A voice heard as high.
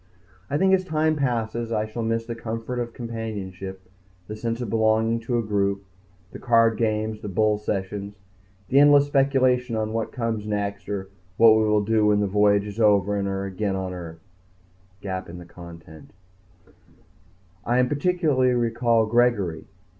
No: low, 110 Hz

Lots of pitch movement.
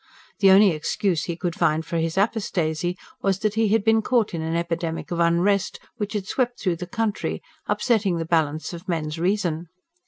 No: average, 3.8 semitones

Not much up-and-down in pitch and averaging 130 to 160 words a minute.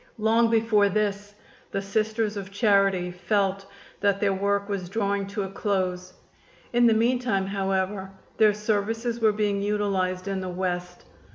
Yes: narrow, 1.9 semitones; average, 150 wpm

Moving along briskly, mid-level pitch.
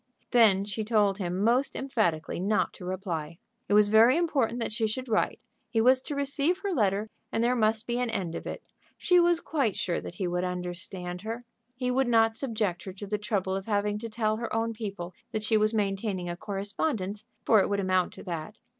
No: fast, 215 wpm; high, 215 Hz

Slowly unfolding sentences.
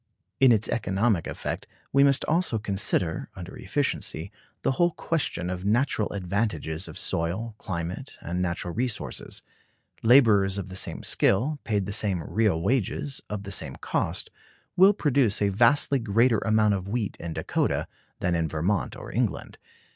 No: average, 155 wpm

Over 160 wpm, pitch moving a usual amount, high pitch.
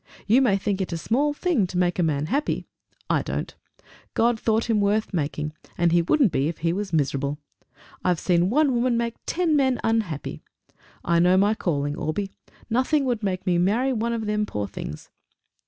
No: average, 190 wpm; wide, 5.7 semitones; high, 200 Hz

